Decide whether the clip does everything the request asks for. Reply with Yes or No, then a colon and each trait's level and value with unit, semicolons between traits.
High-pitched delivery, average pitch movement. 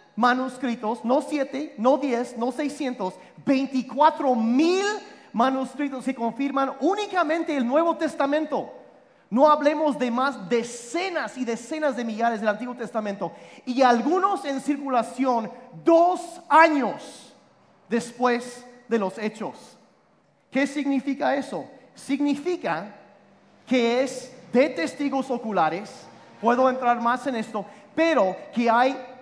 Yes: very high, 260 Hz; average, 3.3 semitones